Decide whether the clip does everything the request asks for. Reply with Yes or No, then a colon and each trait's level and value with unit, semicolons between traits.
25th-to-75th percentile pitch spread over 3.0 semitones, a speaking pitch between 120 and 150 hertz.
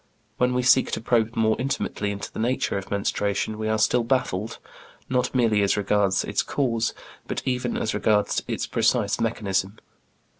No: average, 3.4 semitones; low, 110 Hz